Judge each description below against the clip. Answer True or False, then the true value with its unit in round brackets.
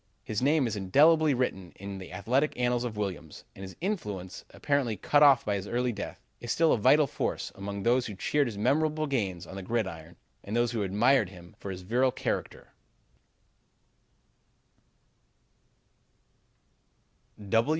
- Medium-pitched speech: False (115 Hz)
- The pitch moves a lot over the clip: True (5.8 semitones)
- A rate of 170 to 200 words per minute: False (150 wpm)